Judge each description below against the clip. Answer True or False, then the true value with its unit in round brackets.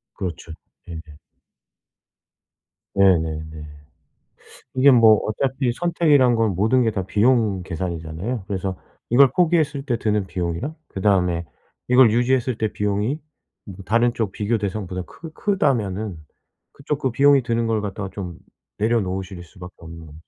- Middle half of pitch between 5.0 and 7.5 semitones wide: True (5.3 semitones)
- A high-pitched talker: False (105 Hz)